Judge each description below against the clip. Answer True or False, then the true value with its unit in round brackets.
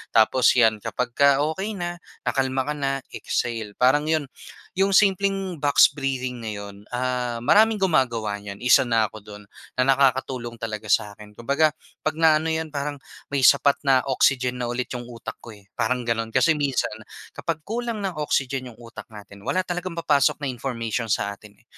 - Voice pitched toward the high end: False (130 Hz)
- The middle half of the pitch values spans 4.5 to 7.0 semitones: True (4.9 semitones)